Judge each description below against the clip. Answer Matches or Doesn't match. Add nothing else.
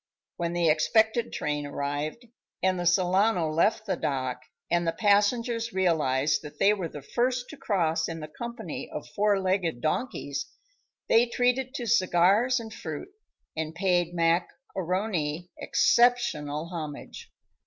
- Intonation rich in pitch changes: Matches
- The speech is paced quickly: Doesn't match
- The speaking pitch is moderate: Matches